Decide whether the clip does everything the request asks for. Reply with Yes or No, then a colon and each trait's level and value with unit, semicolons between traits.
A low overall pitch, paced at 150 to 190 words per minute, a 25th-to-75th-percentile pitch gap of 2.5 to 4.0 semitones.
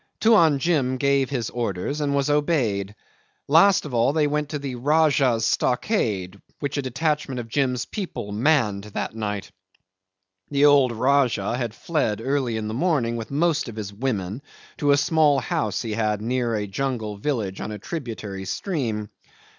No: low, 125 Hz; average, 170 wpm; average, 5.1 semitones